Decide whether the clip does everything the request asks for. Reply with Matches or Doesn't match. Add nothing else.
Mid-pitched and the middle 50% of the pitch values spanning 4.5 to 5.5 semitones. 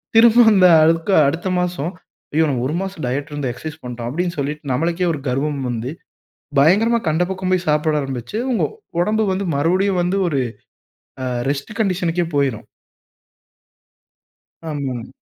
Matches